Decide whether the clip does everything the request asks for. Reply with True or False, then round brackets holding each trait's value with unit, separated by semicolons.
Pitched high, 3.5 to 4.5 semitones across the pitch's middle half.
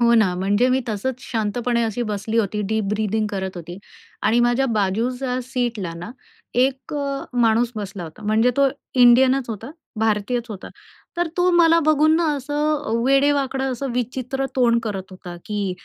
True (235 Hz; 4.2 semitones)